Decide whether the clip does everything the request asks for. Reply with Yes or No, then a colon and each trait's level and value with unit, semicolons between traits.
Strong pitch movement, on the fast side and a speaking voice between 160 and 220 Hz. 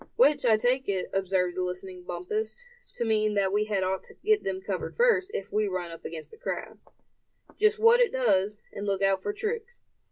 Yes: wide, 7.0 semitones; fast, 210 wpm; high, 205 Hz